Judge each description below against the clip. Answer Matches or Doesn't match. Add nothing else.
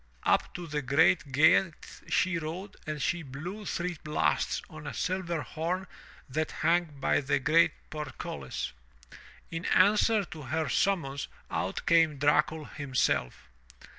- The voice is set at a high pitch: Doesn't match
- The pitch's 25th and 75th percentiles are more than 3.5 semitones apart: Doesn't match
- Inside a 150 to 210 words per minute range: Doesn't match